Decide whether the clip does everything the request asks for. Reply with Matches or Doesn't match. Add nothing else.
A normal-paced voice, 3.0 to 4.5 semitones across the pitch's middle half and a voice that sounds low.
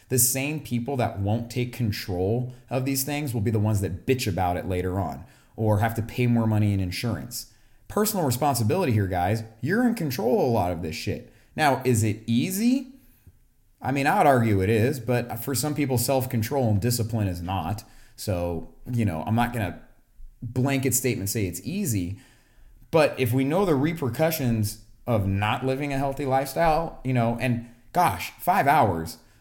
Matches